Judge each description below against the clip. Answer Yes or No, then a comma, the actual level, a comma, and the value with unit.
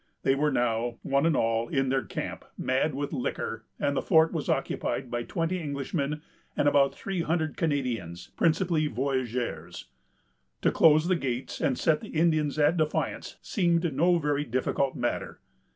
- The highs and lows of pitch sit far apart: No, average, 3.8 semitones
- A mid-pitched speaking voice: Yes, medium, 145 Hz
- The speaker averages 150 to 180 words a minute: Yes, average, 160 wpm